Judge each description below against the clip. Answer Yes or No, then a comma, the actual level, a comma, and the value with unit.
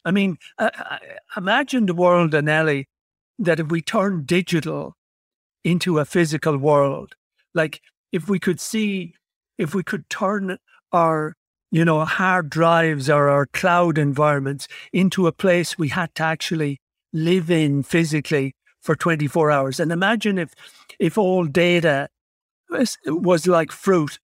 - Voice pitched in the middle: Yes, medium, 170 Hz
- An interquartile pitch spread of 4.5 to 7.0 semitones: No, average, 3.2 semitones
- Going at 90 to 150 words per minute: Yes, average, 140 wpm